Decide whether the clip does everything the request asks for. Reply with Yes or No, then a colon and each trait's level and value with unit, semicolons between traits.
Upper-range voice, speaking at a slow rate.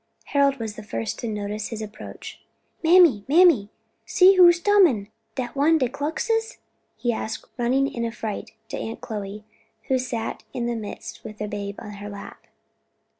No: high, 235 Hz; average, 165 wpm